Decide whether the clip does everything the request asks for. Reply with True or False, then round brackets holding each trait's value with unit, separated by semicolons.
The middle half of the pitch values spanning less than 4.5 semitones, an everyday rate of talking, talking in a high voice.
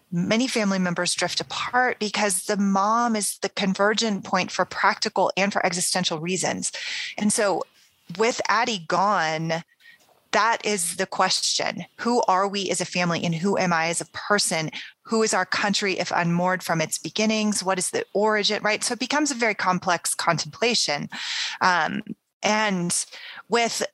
True (3.5 semitones; 160 wpm; 195 Hz)